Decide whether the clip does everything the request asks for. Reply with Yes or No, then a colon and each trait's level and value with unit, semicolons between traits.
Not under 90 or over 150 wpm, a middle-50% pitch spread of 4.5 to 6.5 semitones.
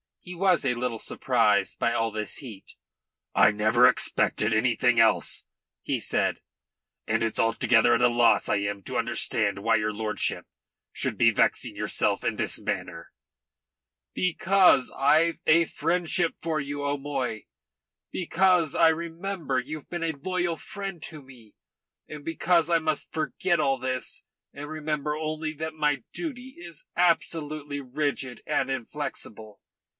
Yes: average, 145 wpm; wide, 5.6 semitones